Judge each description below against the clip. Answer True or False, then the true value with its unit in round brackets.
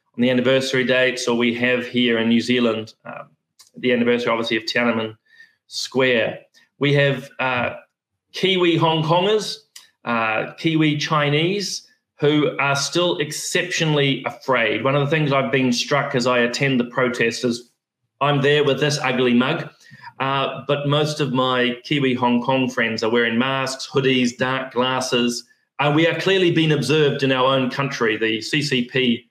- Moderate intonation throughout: True (3.4 semitones)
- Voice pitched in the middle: False (130 Hz)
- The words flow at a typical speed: True (160 wpm)